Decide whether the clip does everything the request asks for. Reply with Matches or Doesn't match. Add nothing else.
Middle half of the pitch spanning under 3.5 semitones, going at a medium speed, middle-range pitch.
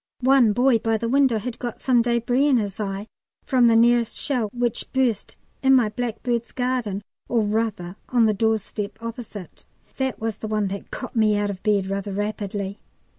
Doesn't match